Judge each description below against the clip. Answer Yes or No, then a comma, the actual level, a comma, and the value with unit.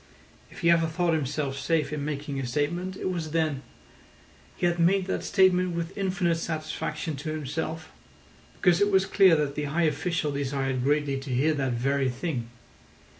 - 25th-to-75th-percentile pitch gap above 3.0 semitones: Yes, average, 3.5 semitones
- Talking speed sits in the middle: Yes, average, 175 wpm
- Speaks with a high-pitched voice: No, medium, 155 Hz